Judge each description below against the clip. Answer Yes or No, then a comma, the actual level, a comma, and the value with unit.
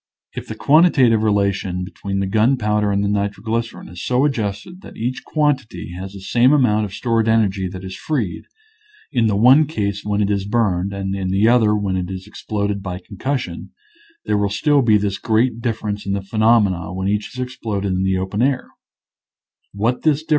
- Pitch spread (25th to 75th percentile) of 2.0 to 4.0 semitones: Yes, average, 3.3 semitones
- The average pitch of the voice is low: Yes, low, 105 Hz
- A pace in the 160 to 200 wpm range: Yes, average, 185 wpm